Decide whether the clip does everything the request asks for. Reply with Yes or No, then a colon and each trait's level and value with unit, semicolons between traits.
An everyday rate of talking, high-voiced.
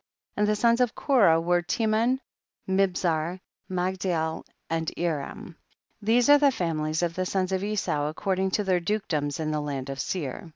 No: average, 170 wpm; medium, 180 Hz